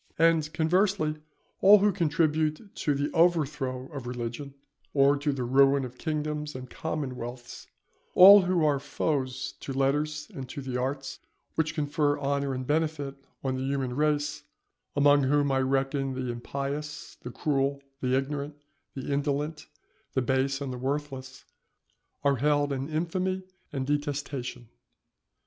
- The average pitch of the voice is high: No, medium, 140 Hz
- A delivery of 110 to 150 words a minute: Yes, average, 140 wpm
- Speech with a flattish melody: Yes, narrow, 2.3 semitones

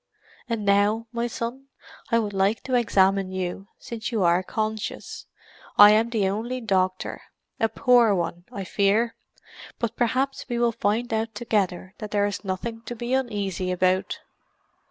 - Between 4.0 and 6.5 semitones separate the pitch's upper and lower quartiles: No, average, 3.3 semitones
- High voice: Yes, high, 215 Hz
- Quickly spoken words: No, average, 155 wpm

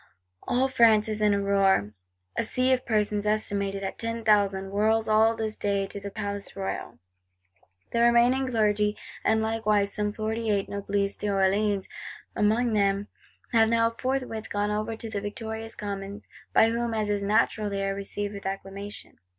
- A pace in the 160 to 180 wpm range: Yes, average, 165 wpm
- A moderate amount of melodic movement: No, narrow, 1.9 semitones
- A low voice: No, high, 210 Hz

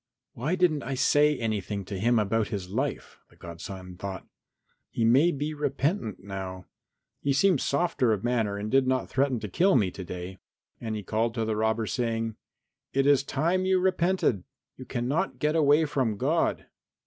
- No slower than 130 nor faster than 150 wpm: No, average, 175 wpm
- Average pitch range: No, wide, 5.8 semitones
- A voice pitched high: No, low, 120 Hz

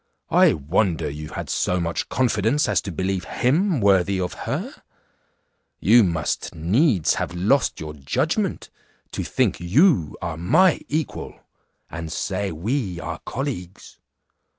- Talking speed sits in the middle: No, slow, 130 wpm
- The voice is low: Yes, very low, 95 Hz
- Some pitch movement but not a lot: No, wide, 6.8 semitones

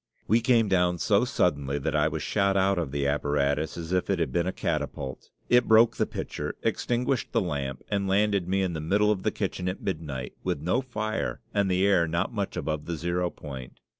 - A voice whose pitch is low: Yes, very low, 90 Hz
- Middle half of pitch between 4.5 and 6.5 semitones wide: Yes, average, 4.9 semitones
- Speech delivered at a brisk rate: Yes, fast, 215 wpm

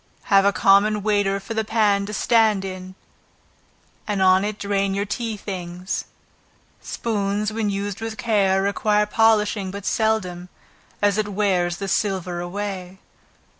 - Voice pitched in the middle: No, high, 200 Hz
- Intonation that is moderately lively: No, narrow, 1.7 semitones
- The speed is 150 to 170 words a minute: No, average, 140 wpm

